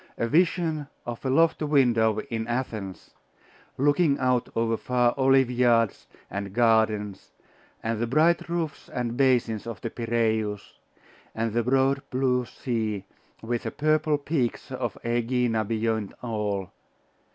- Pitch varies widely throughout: No, average, 3.2 semitones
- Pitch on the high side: No, low, 120 Hz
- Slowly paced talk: Yes, slow, 130 wpm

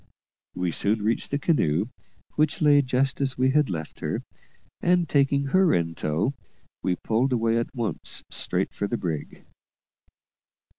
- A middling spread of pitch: No, wide, 6.1 semitones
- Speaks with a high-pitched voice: No, low, 125 Hz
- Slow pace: No, average, 150 wpm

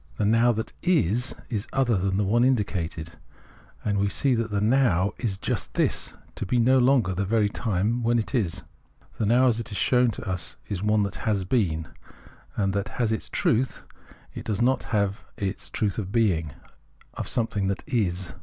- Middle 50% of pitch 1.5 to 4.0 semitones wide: Yes, average, 3.5 semitones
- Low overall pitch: Yes, low, 105 Hz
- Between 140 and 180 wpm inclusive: No, average, 195 wpm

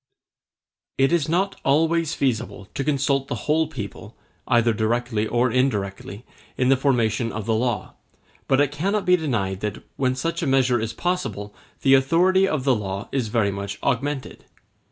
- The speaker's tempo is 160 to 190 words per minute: Yes, average, 165 wpm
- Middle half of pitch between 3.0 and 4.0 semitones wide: No, average, 4.8 semitones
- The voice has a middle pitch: No, low, 130 Hz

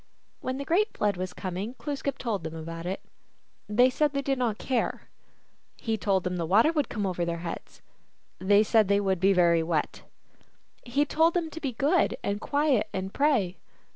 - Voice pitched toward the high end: Yes, high, 210 Hz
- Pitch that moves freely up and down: Yes, wide, 7.1 semitones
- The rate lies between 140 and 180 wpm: No, average, 190 wpm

